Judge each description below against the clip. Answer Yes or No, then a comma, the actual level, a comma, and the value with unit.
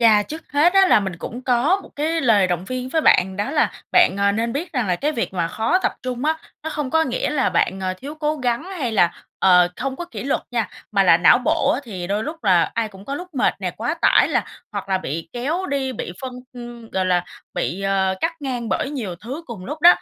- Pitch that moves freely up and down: Yes, wide, 7.3 semitones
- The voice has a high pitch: Yes, high, 240 Hz